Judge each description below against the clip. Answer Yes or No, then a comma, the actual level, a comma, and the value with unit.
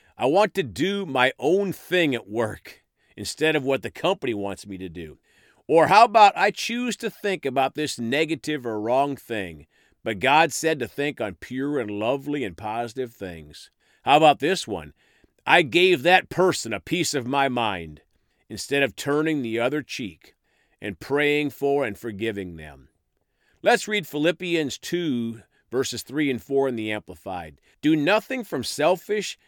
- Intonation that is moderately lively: No, wide, 7.2 semitones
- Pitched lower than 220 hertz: Yes, medium, 140 Hz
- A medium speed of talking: Yes, average, 170 wpm